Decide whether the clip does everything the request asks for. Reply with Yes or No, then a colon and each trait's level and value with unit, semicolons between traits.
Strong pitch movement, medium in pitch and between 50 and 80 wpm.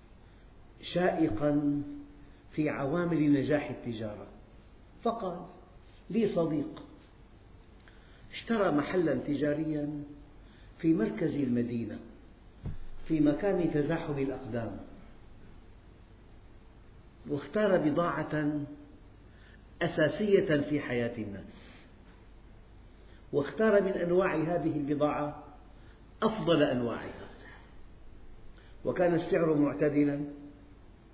Yes: wide, 6.8 semitones; medium, 145 Hz; slow, 65 wpm